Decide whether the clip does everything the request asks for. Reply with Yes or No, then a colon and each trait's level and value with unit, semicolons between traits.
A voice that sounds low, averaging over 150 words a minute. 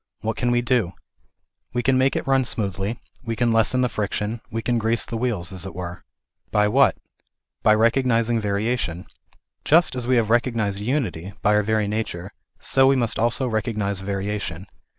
Yes: low, 110 Hz; average, 175 wpm